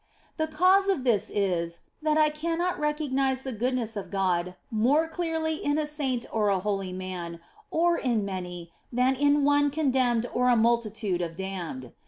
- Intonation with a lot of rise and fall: Yes, wide, 7.5 semitones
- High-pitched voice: Yes, very high, 250 Hz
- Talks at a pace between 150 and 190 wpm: Yes, average, 170 wpm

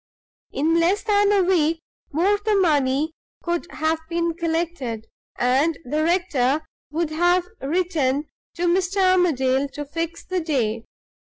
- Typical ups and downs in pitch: Yes, average, 3.7 semitones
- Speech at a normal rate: No, slow, 130 wpm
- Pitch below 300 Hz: No, very high, 330 Hz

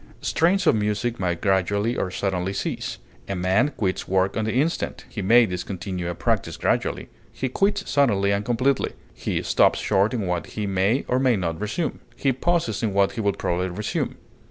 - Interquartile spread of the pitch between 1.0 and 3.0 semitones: No, average, 4.4 semitones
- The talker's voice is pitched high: No, low, 105 Hz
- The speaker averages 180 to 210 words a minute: Yes, average, 185 wpm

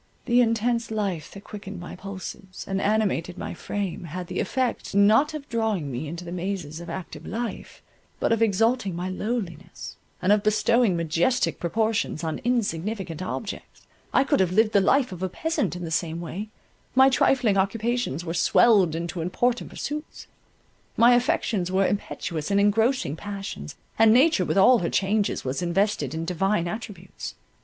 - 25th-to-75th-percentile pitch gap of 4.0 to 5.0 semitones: Yes, average, 4.7 semitones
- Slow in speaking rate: No, average, 160 wpm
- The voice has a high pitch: Yes, high, 200 Hz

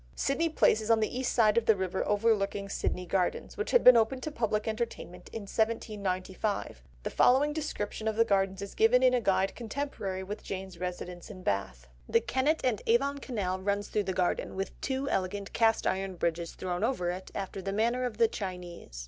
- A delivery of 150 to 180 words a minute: No, average, 200 wpm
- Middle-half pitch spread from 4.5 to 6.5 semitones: No, average, 3.9 semitones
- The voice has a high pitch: Yes, high, 205 Hz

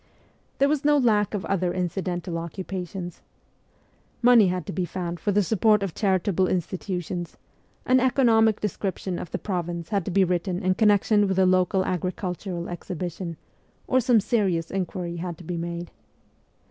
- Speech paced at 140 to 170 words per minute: Yes, average, 160 wpm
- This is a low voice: No, medium, 185 Hz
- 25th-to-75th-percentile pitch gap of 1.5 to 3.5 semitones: Yes, average, 2.9 semitones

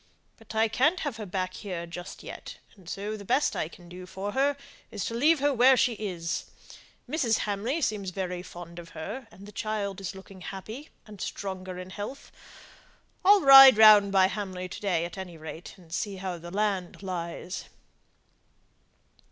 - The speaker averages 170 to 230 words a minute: Yes, average, 180 wpm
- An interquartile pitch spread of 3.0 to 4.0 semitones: Yes, average, 3.5 semitones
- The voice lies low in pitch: No, high, 200 Hz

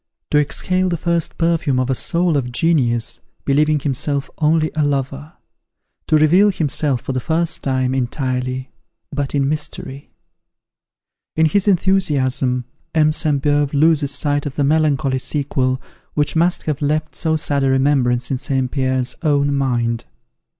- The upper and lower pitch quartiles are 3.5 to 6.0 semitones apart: No, average, 3.0 semitones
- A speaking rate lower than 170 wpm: Yes, average, 150 wpm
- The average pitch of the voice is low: No, medium, 145 Hz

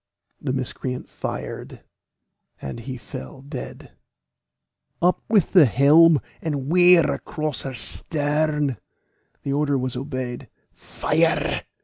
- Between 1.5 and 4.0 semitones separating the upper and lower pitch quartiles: Yes, average, 3.1 semitones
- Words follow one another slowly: Yes, slow, 105 wpm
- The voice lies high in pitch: No, medium, 140 Hz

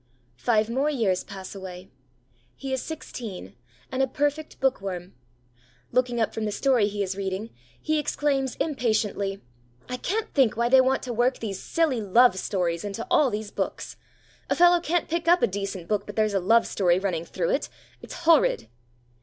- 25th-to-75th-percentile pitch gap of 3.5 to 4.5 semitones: No, wide, 5.5 semitones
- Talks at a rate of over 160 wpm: Yes, average, 180 wpm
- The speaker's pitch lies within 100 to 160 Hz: No, high, 225 Hz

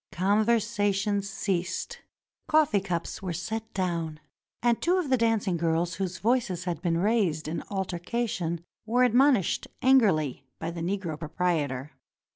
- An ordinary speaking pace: No, slow, 130 wpm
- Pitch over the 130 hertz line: Yes, high, 190 Hz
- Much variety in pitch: No, average, 5.0 semitones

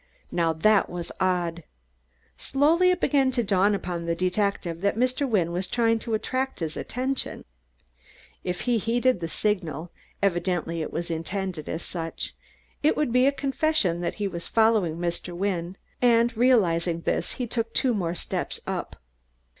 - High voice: Yes, high, 195 Hz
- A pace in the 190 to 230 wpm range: No, average, 160 wpm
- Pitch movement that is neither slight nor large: No, wide, 5.8 semitones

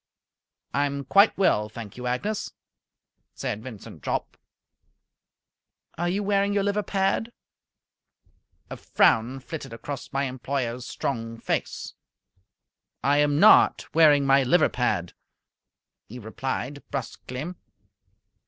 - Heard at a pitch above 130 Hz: Yes, medium, 140 Hz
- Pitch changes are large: Yes, wide, 6.1 semitones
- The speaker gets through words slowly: Yes, slow, 110 wpm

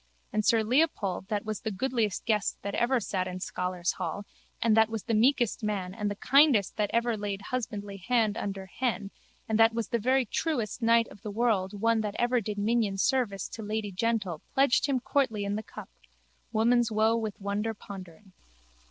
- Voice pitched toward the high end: Yes, high, 215 Hz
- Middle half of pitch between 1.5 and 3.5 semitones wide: Yes, narrow, 2.6 semitones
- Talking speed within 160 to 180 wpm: No, average, 190 wpm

